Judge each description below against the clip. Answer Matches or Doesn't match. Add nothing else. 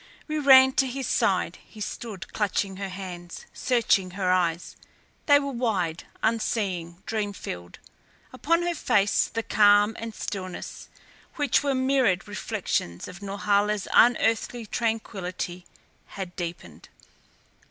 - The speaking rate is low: Matches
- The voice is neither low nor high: Doesn't match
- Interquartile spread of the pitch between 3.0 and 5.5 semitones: Matches